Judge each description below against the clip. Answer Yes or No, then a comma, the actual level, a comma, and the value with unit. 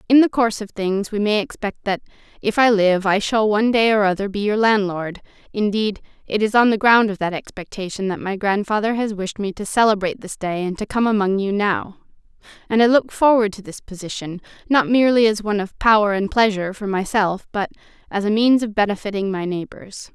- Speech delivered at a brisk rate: Yes, fast, 210 wpm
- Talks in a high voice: Yes, high, 205 Hz